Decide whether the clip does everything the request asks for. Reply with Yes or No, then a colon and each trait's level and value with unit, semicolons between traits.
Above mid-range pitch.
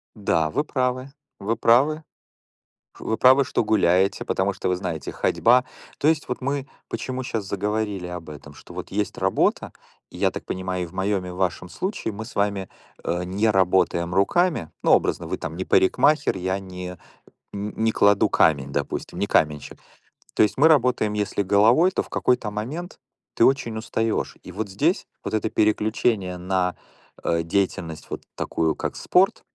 No: low, 100 Hz